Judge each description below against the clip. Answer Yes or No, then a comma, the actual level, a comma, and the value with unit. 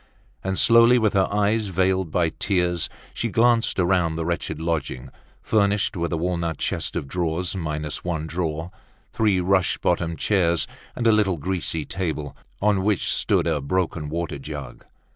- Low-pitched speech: Yes, very low, 90 Hz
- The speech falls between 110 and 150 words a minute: No, average, 160 wpm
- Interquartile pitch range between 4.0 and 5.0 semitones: No, average, 3.3 semitones